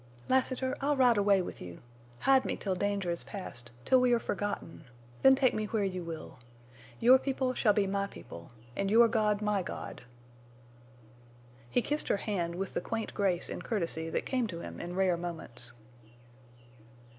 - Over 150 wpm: Yes, average, 170 wpm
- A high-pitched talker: Yes, high, 200 Hz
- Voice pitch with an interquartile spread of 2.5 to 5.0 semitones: No, wide, 5.6 semitones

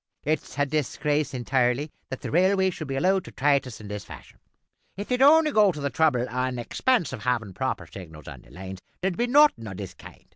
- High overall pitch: No, medium, 140 Hz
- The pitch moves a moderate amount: No, wide, 7.5 semitones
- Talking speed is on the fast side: Yes, fast, 220 wpm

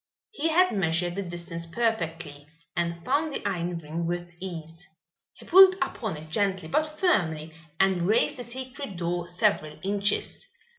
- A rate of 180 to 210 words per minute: No, average, 150 wpm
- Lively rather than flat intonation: Yes, wide, 6.1 semitones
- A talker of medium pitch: Yes, medium, 180 Hz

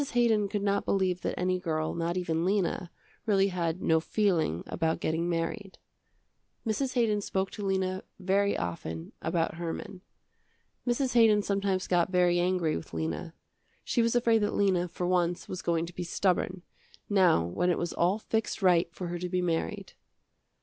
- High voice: No, medium, 180 Hz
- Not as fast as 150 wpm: No, average, 170 wpm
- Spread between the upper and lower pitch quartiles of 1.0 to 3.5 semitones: Yes, average, 3.0 semitones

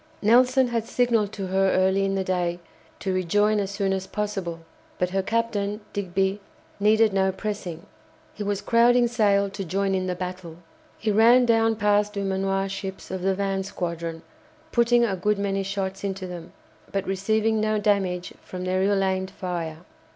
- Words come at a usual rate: Yes, average, 170 wpm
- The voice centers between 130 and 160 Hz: No, high, 195 Hz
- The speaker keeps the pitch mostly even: Yes, narrow, 2.1 semitones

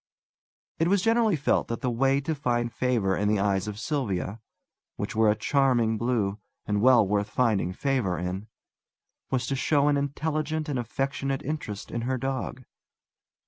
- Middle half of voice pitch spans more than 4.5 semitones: Yes, average, 4.9 semitones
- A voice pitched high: No, low, 125 Hz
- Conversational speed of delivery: Yes, average, 165 wpm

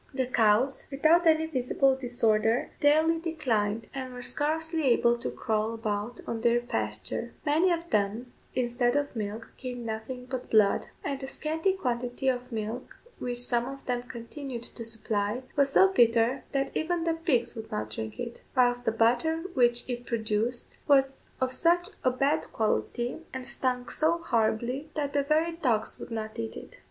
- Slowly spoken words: No, average, 170 wpm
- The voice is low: No, high, 245 Hz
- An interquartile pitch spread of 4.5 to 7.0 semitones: No, average, 3.9 semitones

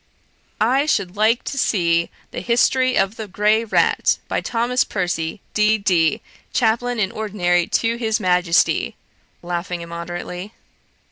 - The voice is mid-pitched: No, high, 205 Hz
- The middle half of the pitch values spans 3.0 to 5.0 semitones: Yes, average, 4.4 semitones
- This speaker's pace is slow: Yes, slow, 125 wpm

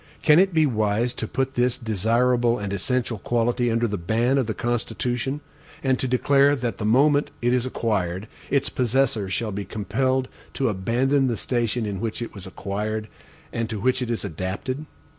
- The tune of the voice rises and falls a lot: No, average, 3.3 semitones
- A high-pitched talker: No, low, 120 Hz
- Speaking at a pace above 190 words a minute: No, average, 180 wpm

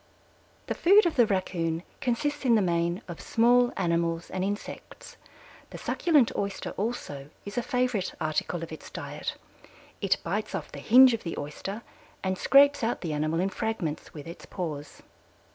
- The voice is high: Yes, high, 195 Hz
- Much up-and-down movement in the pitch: Yes, wide, 6.4 semitones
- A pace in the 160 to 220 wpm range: Yes, average, 165 wpm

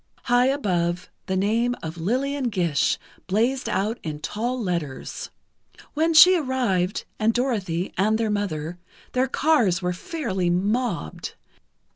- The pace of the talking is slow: Yes, slow, 125 wpm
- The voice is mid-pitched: No, high, 210 Hz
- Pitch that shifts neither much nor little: No, wide, 6.1 semitones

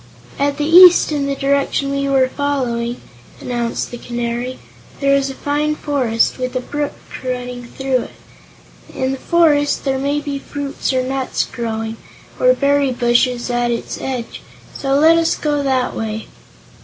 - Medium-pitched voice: No, very high, 270 Hz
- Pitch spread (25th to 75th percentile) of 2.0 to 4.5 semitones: Yes, narrow, 2.6 semitones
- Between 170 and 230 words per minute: No, average, 160 wpm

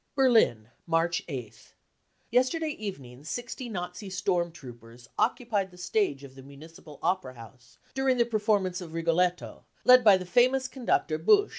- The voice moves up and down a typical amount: No, wide, 8.7 semitones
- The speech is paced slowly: No, average, 160 wpm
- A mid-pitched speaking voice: Yes, medium, 180 Hz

